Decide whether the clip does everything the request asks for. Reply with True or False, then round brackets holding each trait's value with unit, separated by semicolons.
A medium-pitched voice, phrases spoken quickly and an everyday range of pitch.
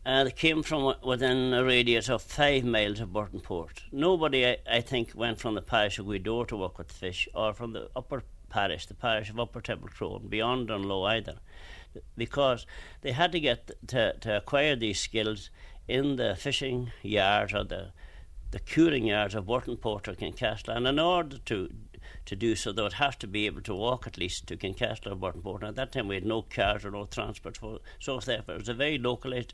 False (115 Hz; 210 wpm; 3.8 semitones)